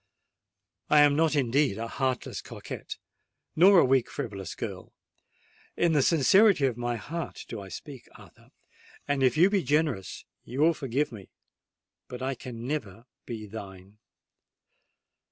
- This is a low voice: Yes, low, 130 Hz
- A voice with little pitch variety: No, average, 4.9 semitones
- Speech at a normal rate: No, slow, 130 wpm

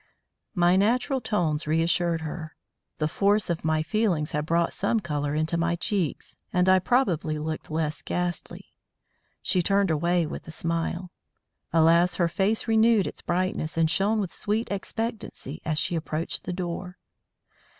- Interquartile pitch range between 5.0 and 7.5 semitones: No, average, 3.7 semitones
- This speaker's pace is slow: No, average, 150 wpm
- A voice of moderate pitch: Yes, medium, 175 Hz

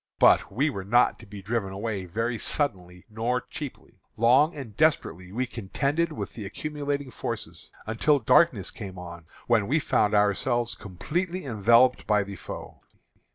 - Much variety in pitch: Yes, wide, 5.9 semitones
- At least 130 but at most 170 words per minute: Yes, average, 155 wpm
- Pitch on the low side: Yes, low, 115 Hz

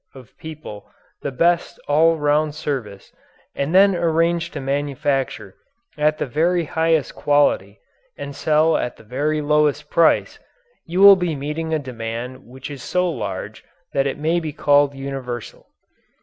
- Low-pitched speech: No, medium, 145 Hz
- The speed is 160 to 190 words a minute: No, average, 150 wpm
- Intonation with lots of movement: No, average, 3.0 semitones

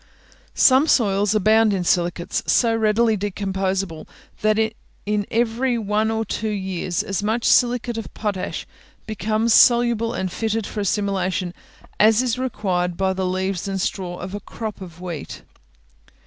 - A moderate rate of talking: Yes, average, 145 wpm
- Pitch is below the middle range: No, high, 210 Hz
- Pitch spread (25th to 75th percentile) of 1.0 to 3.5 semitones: Yes, average, 3.0 semitones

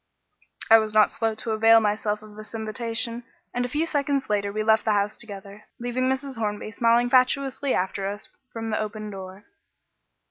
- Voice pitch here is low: No, high, 220 Hz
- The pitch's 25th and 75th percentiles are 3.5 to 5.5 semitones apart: No, narrow, 2.6 semitones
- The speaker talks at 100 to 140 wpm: No, average, 180 wpm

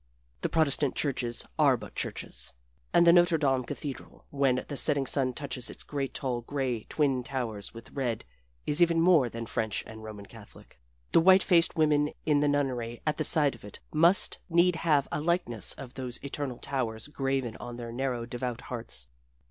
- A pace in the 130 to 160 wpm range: No, average, 180 wpm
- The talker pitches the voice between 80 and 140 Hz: Yes, low, 135 Hz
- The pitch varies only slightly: No, average, 4.0 semitones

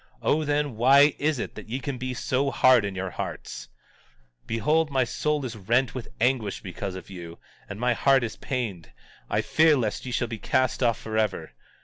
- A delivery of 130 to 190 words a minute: No, average, 200 wpm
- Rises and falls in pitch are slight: No, average, 4.1 semitones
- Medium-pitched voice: No, low, 125 Hz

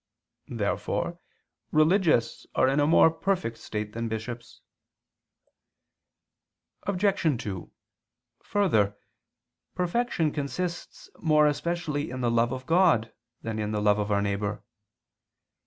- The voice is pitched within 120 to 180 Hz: Yes, low, 135 Hz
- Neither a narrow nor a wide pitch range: No, wide, 7.6 semitones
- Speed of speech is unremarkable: No, slow, 110 wpm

